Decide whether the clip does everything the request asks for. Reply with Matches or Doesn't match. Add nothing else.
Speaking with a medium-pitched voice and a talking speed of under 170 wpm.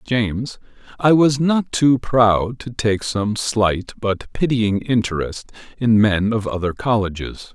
Doesn't match